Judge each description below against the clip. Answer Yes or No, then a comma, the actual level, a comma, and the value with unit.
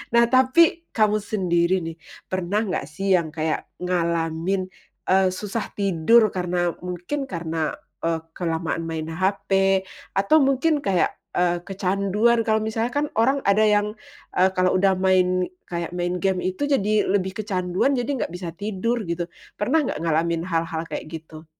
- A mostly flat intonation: No, average, 3.8 semitones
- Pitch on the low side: No, medium, 185 Hz